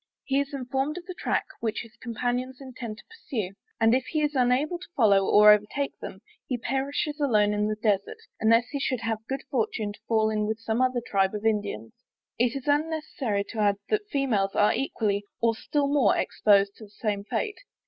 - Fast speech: Yes, fast, 210 wpm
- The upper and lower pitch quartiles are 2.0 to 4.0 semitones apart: No, average, 4.5 semitones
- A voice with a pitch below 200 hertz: No, high, 230 Hz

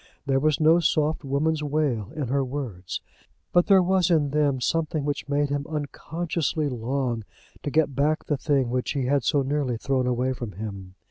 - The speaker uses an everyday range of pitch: Yes, average, 3.2 semitones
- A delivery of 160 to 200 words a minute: Yes, average, 185 wpm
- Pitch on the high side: No, medium, 140 Hz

